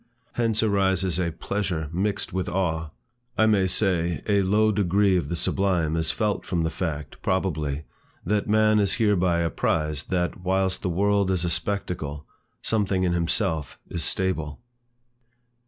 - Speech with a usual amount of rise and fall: Yes, average, 3.3 semitones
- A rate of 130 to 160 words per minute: Yes, average, 150 wpm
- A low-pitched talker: Yes, very low, 95 Hz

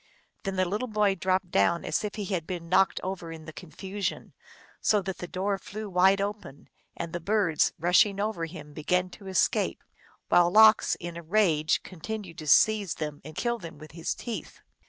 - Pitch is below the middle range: No, medium, 185 Hz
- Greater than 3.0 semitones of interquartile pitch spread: Yes, average, 3.6 semitones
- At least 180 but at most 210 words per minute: Yes, average, 185 wpm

